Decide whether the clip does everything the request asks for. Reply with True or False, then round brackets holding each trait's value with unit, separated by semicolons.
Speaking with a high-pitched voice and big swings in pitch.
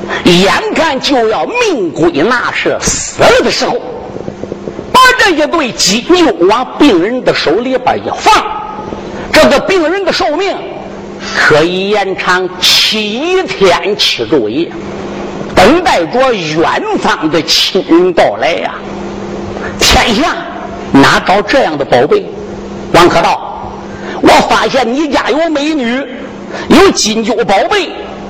True (300 Hz; 8.3 semitones)